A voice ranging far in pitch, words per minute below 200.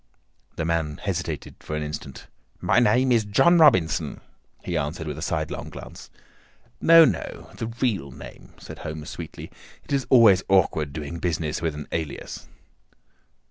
Yes: wide, 6.8 semitones; average, 150 wpm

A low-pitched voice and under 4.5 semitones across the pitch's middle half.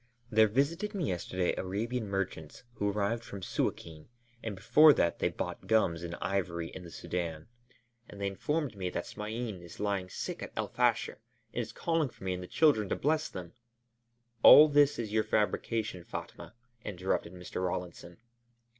No: low, 105 Hz; average, 4.8 semitones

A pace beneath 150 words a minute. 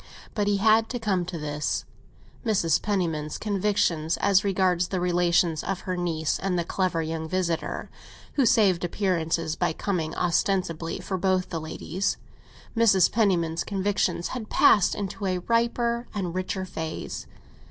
Yes: average, 140 wpm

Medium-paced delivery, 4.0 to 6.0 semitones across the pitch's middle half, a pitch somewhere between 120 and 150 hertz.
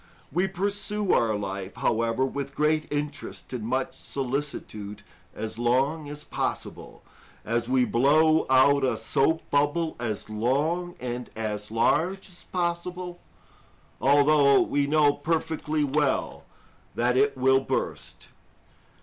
No: slow, 120 wpm; average, 4.6 semitones; medium, 140 Hz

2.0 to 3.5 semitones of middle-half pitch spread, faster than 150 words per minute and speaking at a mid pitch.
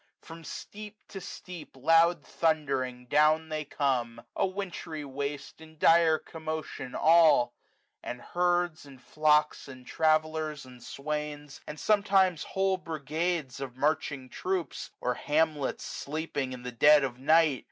No: average, 3.2 semitones; slow, 135 wpm; medium, 155 Hz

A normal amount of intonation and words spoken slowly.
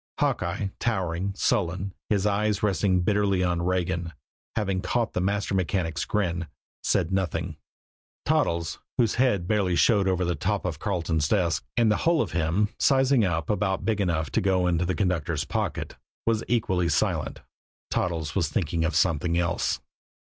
No: average, 3.3 semitones; average, 155 wpm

